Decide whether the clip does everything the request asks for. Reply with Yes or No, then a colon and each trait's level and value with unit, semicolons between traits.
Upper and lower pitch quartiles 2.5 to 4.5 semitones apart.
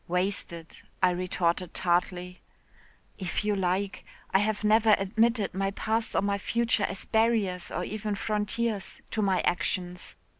Yes: average, 2.9 semitones